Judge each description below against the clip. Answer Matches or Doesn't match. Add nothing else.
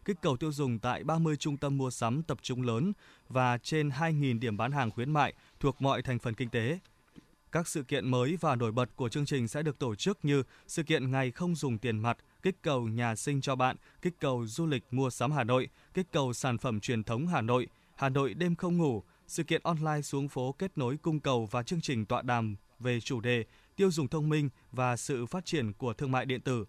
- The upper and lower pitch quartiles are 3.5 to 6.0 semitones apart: Matches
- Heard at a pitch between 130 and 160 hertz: Matches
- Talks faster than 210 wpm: Matches